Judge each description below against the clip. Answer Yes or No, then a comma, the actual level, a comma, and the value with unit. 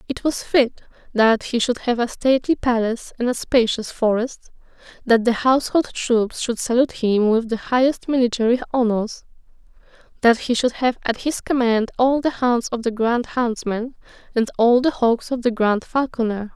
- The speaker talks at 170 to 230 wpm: Yes, average, 175 wpm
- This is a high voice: Yes, high, 240 Hz